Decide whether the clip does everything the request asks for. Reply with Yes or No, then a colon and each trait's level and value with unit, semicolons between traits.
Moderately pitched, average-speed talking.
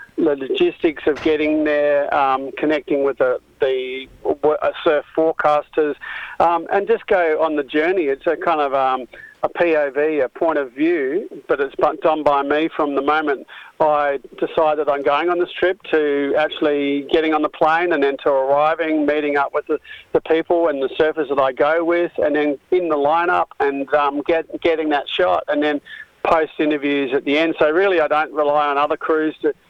Yes: medium, 155 Hz; average, 195 wpm